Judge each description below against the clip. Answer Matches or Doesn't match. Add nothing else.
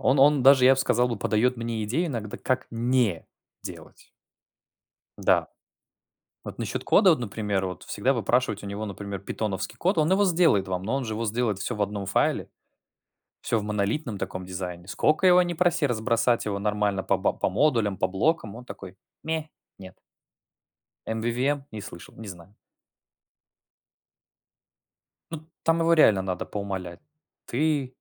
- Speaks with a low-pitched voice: Matches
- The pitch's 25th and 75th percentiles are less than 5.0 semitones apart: Doesn't match